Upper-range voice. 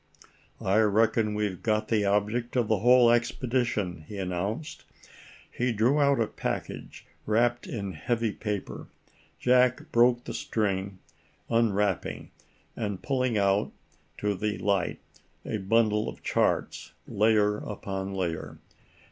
No: low, 105 Hz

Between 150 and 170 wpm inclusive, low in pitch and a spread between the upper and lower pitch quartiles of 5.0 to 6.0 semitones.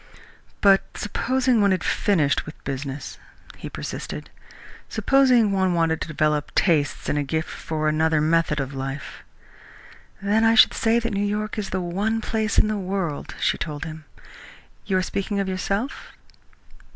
No: average, 160 wpm; medium, 185 Hz; wide, 5.5 semitones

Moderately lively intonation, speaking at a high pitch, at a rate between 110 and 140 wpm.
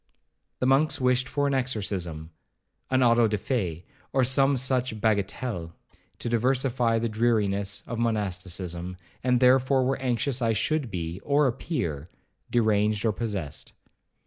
No: average, 4.5 semitones; low, 115 Hz; slow, 135 wpm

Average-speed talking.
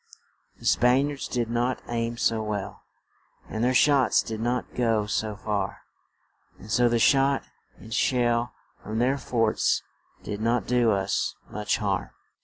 Yes: average, 150 wpm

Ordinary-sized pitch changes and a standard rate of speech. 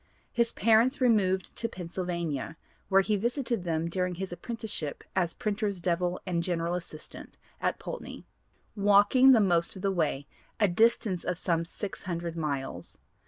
Yes: average, 4.0 semitones; average, 145 wpm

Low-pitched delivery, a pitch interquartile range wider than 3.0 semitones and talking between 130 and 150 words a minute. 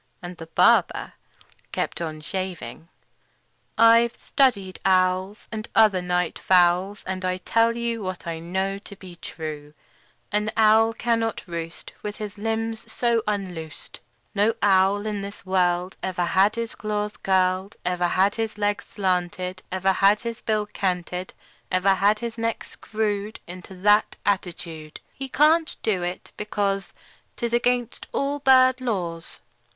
No: high, 200 Hz; average, 3.4 semitones; average, 145 wpm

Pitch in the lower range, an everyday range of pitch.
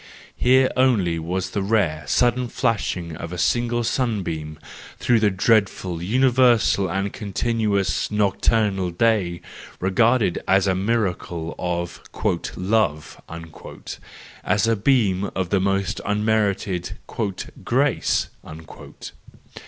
Yes: low, 100 Hz; average, 4.0 semitones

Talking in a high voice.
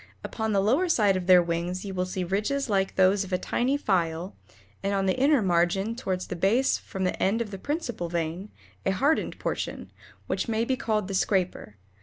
Yes: high, 195 Hz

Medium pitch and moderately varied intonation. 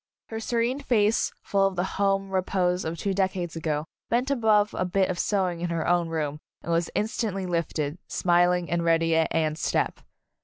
Yes: medium, 180 Hz; average, 3.1 semitones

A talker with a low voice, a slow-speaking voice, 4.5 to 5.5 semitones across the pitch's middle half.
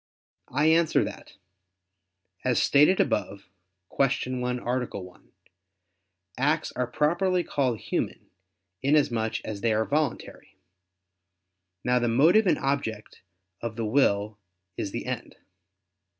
Yes: low, 125 Hz; slow, 115 wpm; average, 4.9 semitones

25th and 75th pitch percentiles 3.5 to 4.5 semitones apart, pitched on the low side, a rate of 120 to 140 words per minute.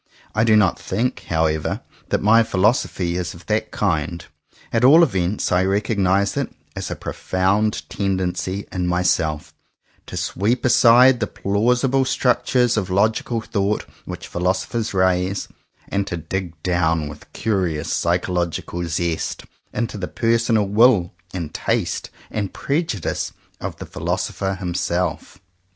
Yes: average, 3.9 semitones; very low, 95 Hz; slow, 135 wpm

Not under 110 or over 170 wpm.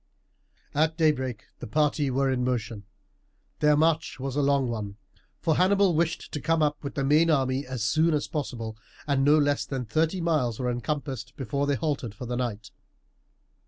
No: average, 180 wpm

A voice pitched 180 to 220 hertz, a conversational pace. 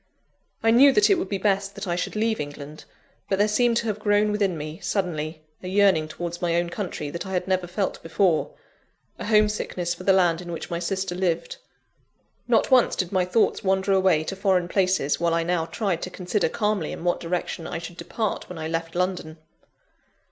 No: medium, 185 Hz; fast, 210 wpm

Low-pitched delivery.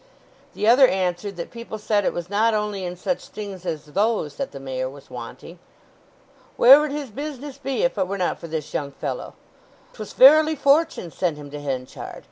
No: high, 205 Hz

